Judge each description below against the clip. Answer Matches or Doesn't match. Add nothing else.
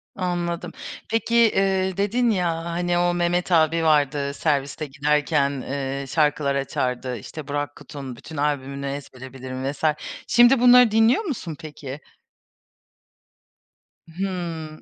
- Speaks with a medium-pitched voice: Matches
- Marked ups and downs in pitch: Doesn't match